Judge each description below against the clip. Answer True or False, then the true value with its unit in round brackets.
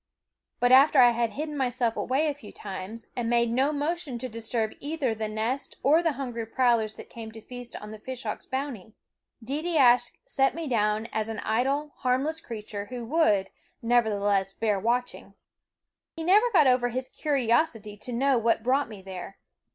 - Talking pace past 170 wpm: True (180 wpm)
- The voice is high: True (245 Hz)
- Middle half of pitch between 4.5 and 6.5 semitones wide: False (3.9 semitones)